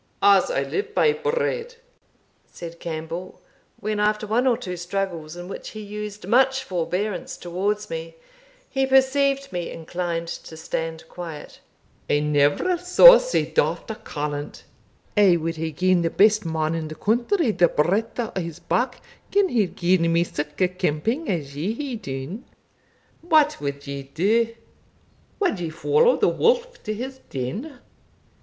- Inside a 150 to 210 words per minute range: Yes, average, 155 wpm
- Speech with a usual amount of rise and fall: No, wide, 8.0 semitones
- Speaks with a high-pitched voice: Yes, high, 195 Hz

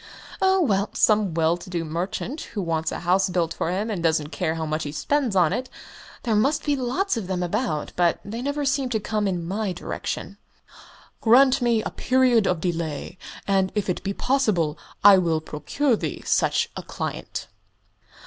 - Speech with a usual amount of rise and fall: No, wide, 6.3 semitones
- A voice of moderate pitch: No, high, 195 Hz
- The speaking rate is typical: Yes, average, 185 wpm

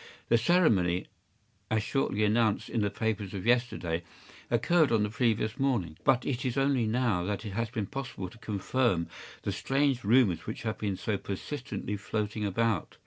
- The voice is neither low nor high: No, low, 110 Hz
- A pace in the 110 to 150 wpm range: No, average, 170 wpm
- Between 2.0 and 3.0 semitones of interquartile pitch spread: No, average, 3.6 semitones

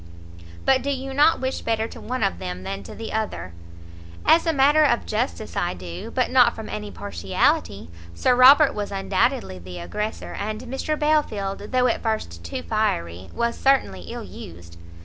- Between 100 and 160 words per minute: No, average, 175 wpm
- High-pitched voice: Yes, high, 215 Hz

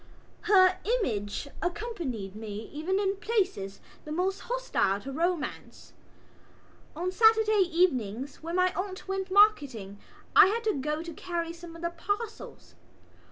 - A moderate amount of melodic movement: No, wide, 6.0 semitones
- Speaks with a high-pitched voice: Yes, very high, 350 Hz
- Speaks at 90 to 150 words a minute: Yes, slow, 135 wpm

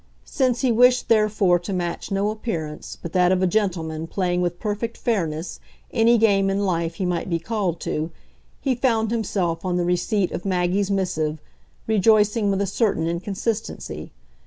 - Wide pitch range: No, average, 3.8 semitones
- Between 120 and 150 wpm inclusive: No, average, 165 wpm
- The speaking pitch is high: Yes, high, 195 Hz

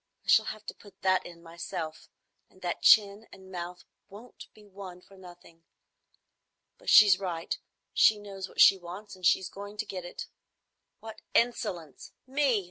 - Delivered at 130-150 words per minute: No, average, 165 wpm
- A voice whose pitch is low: No, high, 190 Hz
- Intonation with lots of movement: No, average, 2.9 semitones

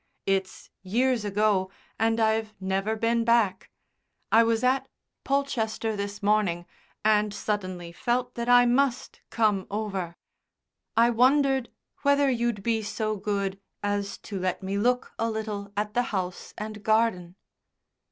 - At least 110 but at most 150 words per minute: Yes, slow, 135 wpm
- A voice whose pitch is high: Yes, high, 215 Hz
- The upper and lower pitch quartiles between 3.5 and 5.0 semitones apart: No, average, 2.9 semitones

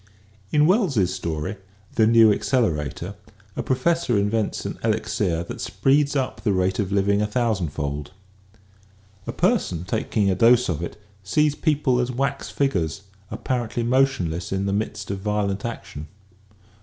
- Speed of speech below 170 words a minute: Yes, average, 150 wpm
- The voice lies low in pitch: Yes, low, 105 Hz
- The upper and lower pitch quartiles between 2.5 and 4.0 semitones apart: No, wide, 5.4 semitones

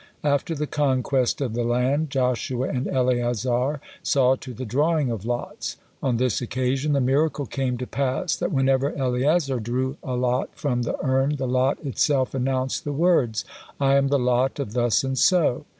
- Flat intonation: Yes, narrow, 2.1 semitones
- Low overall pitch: Yes, low, 130 Hz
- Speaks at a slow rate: No, average, 175 wpm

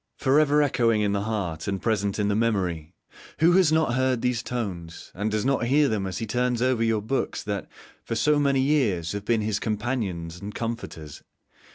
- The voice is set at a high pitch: No, low, 110 Hz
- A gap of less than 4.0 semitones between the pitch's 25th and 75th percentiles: No, average, 4.4 semitones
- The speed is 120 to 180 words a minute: No, average, 200 wpm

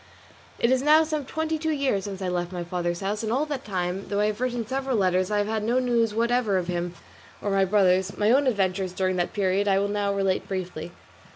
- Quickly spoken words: Yes, fast, 245 wpm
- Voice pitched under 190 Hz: No, high, 205 Hz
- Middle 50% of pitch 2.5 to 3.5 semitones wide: No, average, 4.7 semitones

